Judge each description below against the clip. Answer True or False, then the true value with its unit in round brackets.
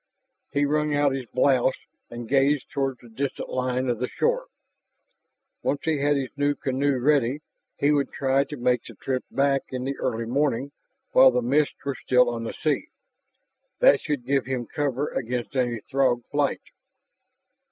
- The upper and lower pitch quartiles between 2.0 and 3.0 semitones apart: True (2.4 semitones)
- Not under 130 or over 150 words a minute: False (170 wpm)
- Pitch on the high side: False (135 Hz)